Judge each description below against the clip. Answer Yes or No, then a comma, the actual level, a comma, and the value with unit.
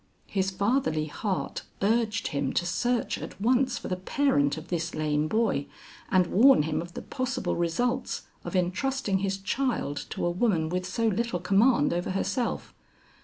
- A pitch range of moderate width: No, wide, 5.7 semitones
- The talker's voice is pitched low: No, high, 195 Hz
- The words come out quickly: No, average, 165 wpm